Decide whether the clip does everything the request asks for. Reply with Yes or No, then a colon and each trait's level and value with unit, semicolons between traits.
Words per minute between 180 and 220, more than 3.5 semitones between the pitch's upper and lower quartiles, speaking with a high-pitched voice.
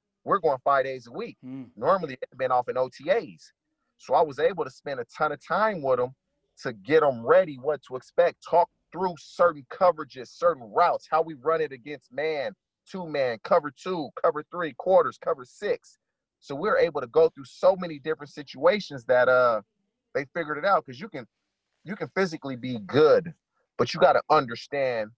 No: average, 190 wpm; wide, 5.5 semitones; medium, 155 Hz